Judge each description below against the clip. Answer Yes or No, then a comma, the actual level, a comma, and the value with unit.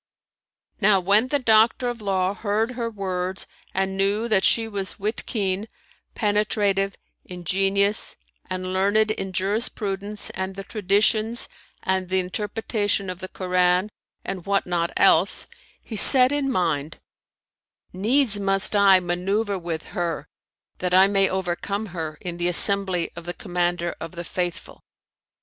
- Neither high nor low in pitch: No, high, 195 Hz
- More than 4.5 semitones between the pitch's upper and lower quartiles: No, narrow, 2.6 semitones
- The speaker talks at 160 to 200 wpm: No, average, 145 wpm